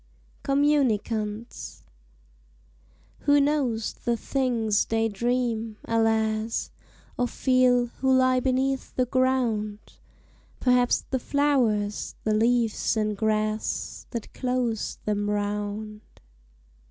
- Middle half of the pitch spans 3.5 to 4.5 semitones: No, average, 3.1 semitones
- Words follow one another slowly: Yes, slow, 90 wpm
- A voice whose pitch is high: Yes, high, 230 Hz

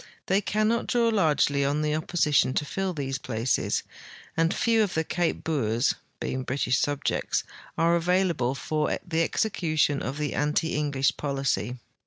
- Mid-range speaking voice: Yes, medium, 150 Hz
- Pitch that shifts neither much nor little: Yes, average, 4.1 semitones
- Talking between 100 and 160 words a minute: Yes, average, 150 wpm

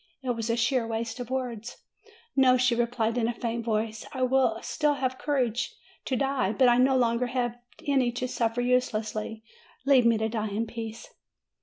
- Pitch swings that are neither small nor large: No, narrow, 2.0 semitones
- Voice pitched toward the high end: Yes, high, 240 Hz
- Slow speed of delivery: No, average, 185 wpm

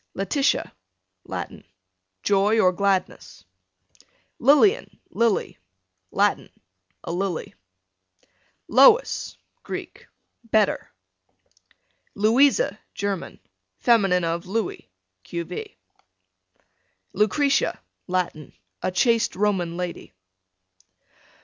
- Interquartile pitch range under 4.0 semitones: No, average, 4.6 semitones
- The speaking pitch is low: No, high, 205 Hz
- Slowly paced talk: Yes, slow, 70 wpm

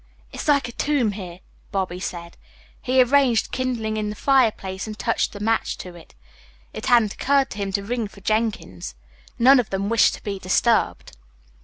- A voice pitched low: No, high, 215 Hz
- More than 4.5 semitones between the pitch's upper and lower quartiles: No, average, 4.1 semitones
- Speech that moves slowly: No, average, 180 wpm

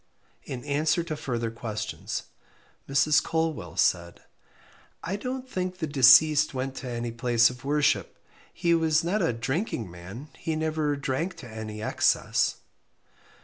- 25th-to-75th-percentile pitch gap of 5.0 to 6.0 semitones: Yes, average, 5.3 semitones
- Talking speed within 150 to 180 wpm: No, average, 140 wpm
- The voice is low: No, medium, 145 Hz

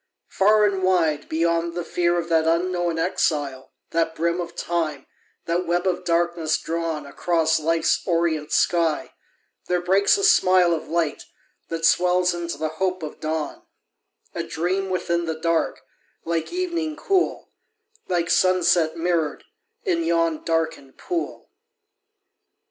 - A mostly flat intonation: Yes, narrow, 1.8 semitones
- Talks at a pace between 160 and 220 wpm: No, slow, 135 wpm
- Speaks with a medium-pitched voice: Yes, medium, 170 Hz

